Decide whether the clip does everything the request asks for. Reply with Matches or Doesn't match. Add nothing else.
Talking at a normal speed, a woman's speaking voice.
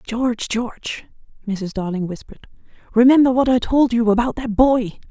Matches